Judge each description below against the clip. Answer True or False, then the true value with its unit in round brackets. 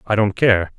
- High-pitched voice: False (105 Hz)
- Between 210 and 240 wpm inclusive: True (230 wpm)